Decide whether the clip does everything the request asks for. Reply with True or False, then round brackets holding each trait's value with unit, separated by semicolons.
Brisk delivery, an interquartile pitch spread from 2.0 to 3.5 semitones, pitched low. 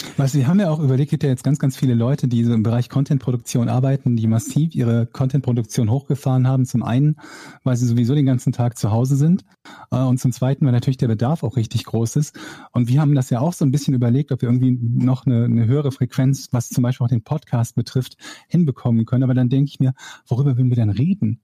True (240 wpm; 2.5 semitones; 130 Hz)